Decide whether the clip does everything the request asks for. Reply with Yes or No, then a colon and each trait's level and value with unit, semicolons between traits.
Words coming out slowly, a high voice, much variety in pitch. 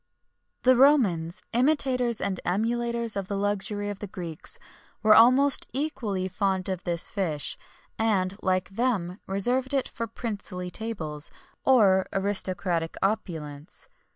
No: slow, 130 wpm; high, 200 Hz; average, 4.3 semitones